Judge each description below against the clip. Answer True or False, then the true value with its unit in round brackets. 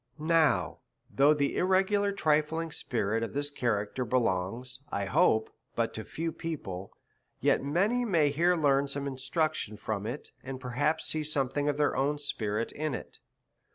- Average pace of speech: True (155 wpm)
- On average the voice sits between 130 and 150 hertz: True (140 Hz)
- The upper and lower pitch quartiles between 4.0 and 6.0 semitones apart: True (5.2 semitones)